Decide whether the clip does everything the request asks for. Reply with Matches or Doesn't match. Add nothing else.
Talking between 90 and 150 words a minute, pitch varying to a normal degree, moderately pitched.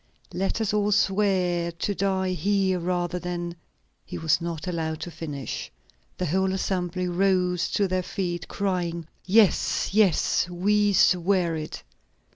Doesn't match